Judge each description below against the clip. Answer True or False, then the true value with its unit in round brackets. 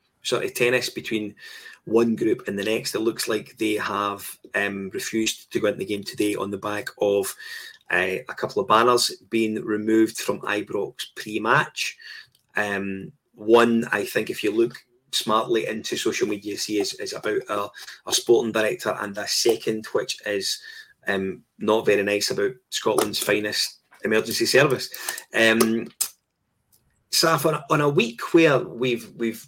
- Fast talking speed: False (160 wpm)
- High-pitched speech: False (115 Hz)